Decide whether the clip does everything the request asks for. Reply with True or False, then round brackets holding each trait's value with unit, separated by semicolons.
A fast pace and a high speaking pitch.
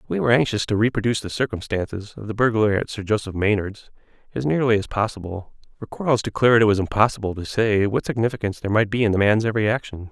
False (215 wpm; 105 Hz)